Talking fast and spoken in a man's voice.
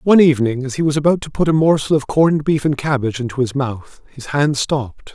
Yes: fast, 245 wpm; male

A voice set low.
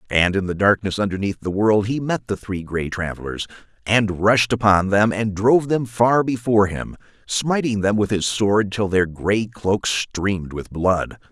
Yes: low, 105 Hz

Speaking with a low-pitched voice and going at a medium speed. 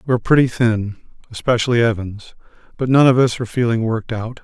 Yes: low, 115 Hz; average, 190 wpm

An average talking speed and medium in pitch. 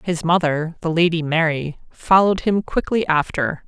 Yes: average, 145 wpm; medium, 165 Hz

